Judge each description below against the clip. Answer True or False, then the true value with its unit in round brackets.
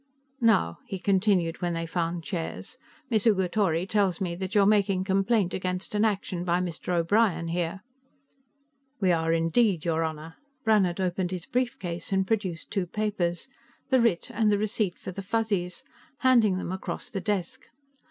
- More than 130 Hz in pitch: True (190 Hz)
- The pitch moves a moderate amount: True (3.3 semitones)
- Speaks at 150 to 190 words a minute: True (160 wpm)